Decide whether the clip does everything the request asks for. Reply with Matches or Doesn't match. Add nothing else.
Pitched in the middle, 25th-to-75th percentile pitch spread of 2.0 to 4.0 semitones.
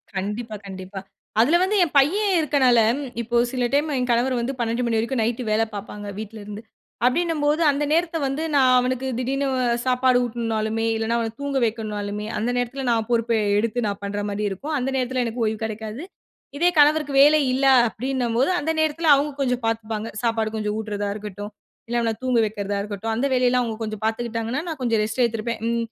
Doesn't match